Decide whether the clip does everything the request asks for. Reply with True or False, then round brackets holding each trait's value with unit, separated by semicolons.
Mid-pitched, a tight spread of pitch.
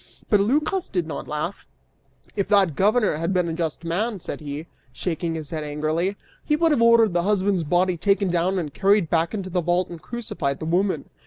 False (180 Hz; 3.8 semitones)